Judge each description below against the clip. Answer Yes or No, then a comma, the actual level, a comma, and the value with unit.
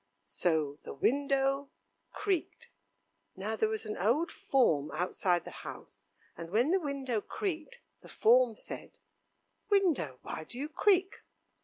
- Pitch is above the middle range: Yes, very high, 255 Hz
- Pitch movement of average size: No, wide, 8.5 semitones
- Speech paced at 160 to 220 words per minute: No, slow, 135 wpm